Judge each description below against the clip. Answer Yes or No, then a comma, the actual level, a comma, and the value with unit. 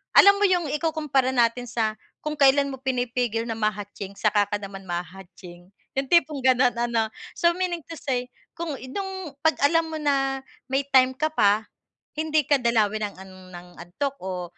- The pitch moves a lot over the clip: Yes, wide, 6.1 semitones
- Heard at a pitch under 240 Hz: No, very high, 255 Hz